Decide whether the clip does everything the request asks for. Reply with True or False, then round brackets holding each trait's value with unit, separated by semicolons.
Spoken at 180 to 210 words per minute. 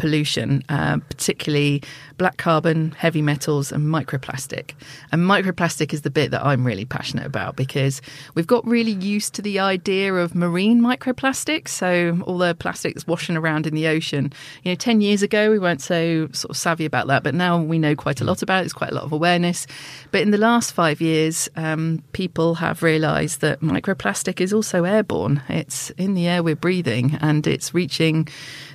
True (190 wpm)